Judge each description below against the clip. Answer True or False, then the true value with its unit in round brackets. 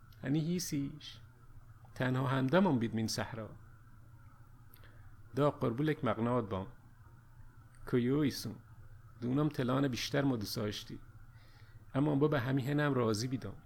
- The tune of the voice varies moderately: True (3.2 semitones)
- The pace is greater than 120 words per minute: False (110 wpm)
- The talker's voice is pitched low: True (115 Hz)